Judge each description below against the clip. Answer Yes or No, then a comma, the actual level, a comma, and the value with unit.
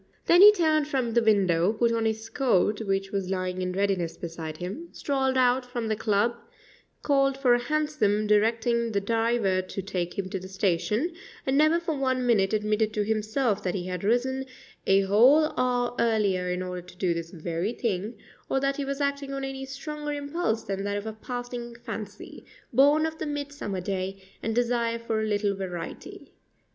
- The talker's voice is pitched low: No, high, 225 Hz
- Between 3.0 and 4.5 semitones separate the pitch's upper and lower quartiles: No, average, 5.3 semitones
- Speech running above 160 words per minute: Yes, average, 190 wpm